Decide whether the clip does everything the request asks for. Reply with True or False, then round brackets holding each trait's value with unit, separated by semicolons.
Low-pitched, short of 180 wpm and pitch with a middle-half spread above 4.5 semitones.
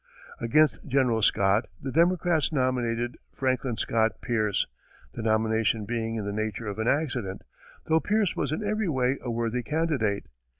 True (120 Hz; 155 wpm; 4.9 semitones)